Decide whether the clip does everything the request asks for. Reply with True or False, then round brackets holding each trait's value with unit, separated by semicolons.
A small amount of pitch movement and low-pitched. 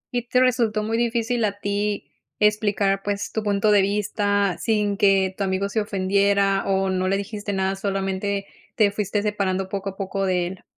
False (1.4 semitones; 200 Hz)